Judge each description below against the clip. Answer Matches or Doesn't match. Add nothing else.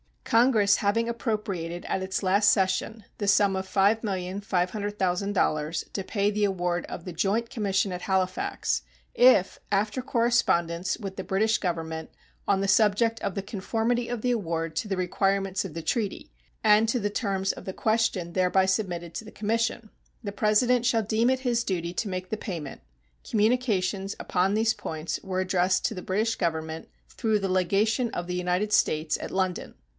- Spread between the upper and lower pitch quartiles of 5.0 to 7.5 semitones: Doesn't match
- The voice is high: Matches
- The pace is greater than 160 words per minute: Matches